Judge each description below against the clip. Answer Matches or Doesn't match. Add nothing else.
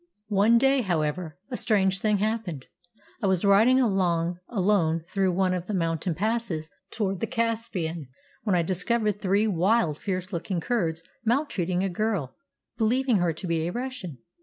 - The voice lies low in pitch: Doesn't match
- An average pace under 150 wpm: Doesn't match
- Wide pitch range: Doesn't match